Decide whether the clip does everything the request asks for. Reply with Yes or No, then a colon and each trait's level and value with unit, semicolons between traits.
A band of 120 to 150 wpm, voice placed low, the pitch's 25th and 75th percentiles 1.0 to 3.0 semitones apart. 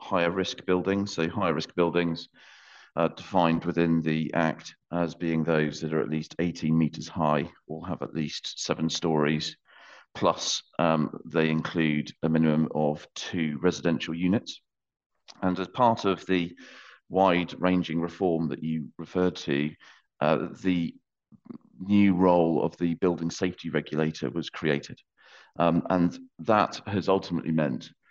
Yes: average, 145 wpm; very low, 85 Hz; narrow, 2.4 semitones